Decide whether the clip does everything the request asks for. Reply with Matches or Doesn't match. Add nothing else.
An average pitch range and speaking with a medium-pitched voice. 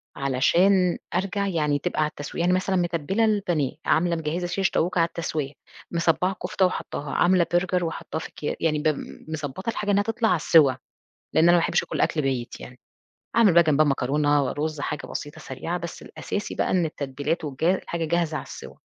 Matches